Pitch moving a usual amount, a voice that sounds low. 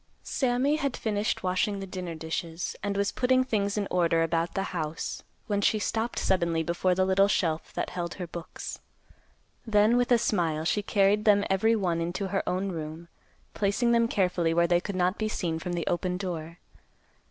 No: average, 3.5 semitones; medium, 185 Hz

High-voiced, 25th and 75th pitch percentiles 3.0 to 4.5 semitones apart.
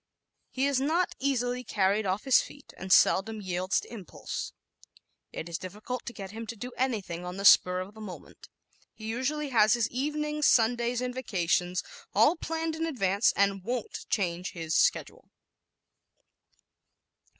No: high, 225 Hz; wide, 5.4 semitones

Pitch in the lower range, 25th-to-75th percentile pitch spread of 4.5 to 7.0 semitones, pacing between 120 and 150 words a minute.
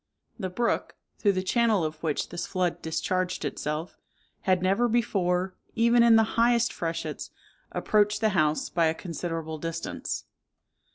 No: medium, 185 Hz; average, 5.0 semitones; average, 145 wpm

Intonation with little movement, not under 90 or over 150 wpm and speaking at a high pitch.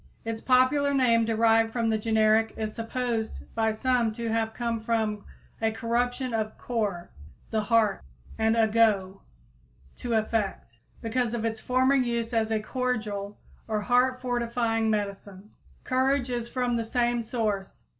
Yes: narrow, 2.0 semitones; average, 145 wpm; high, 225 Hz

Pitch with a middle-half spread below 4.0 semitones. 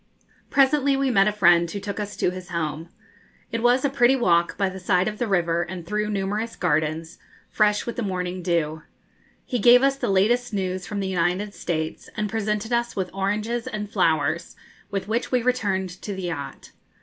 No: average, 4.3 semitones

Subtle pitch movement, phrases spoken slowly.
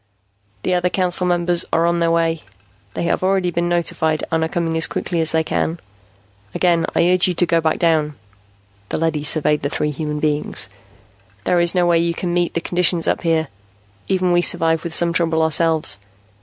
No: narrow, 1.5 semitones; average, 195 wpm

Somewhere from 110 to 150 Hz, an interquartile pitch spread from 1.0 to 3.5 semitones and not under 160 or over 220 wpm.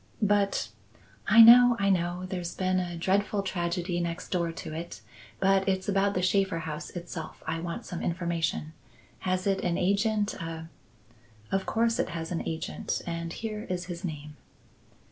No: medium, 175 Hz; average, 2.7 semitones; average, 170 wpm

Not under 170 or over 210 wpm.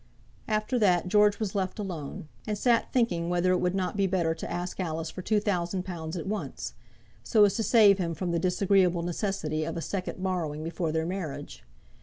Yes: average, 200 wpm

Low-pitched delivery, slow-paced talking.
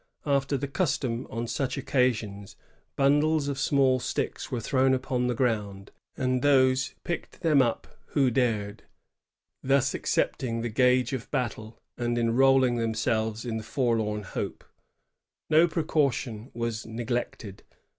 Yes: low, 125 Hz; slow, 130 wpm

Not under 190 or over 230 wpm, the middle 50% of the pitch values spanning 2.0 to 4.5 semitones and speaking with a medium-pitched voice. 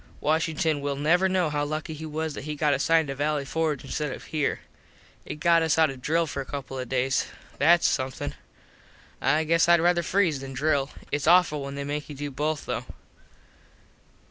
Yes: average, 195 wpm; narrow, 2.5 semitones; medium, 150 Hz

